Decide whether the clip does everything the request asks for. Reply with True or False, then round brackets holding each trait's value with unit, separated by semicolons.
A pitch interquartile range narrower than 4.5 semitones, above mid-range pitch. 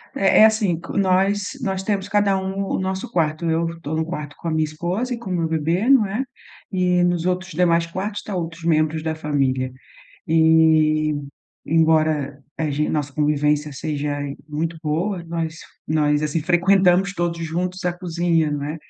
False (3.3 semitones; 165 Hz)